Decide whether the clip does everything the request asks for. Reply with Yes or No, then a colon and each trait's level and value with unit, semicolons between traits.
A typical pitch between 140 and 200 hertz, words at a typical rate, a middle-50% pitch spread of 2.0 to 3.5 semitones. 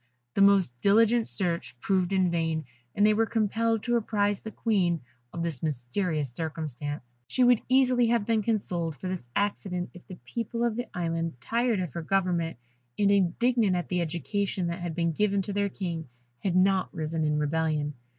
No: medium, 185 Hz; average, 180 wpm; average, 4.3 semitones